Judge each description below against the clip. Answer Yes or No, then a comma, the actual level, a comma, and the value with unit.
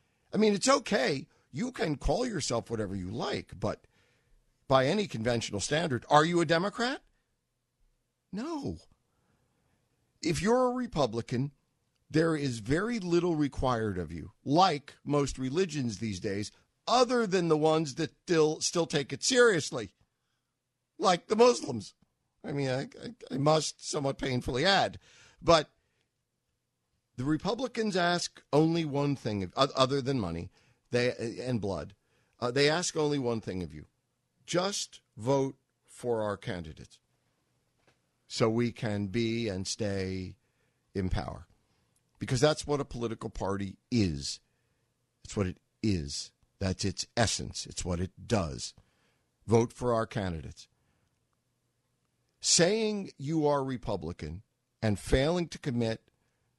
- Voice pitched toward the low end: Yes, low, 130 Hz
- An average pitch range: No, wide, 5.9 semitones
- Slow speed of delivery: Yes, slow, 130 wpm